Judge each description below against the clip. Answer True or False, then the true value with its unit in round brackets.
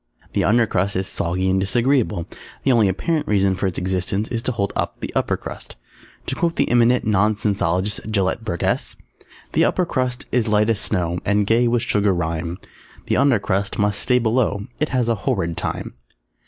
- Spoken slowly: False (185 wpm)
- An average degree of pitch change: True (3.9 semitones)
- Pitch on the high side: False (105 Hz)